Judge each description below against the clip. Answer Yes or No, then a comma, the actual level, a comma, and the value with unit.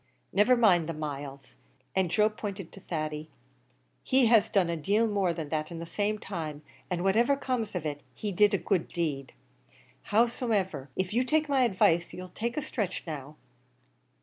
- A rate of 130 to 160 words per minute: No, average, 180 wpm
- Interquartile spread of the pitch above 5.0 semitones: Yes, wide, 5.4 semitones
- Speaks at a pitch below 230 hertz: Yes, medium, 185 Hz